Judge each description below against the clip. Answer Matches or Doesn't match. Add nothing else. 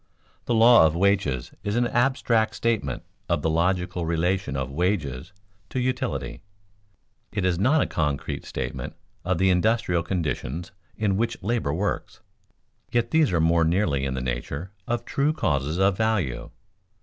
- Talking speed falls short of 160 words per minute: Matches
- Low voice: Matches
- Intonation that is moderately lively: Doesn't match